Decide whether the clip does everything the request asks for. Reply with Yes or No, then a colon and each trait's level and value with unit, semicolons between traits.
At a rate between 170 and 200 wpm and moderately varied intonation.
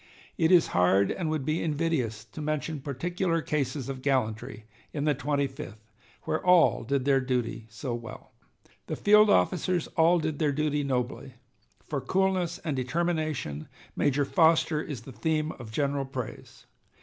No: average, 155 wpm; average, 4.1 semitones